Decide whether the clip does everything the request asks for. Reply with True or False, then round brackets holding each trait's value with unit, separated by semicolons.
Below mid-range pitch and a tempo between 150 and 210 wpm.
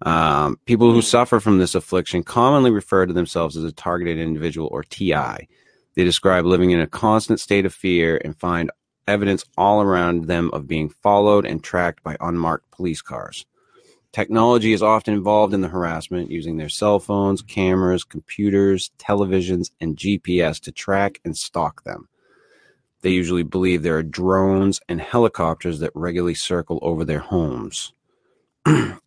True (90 Hz; 155 wpm)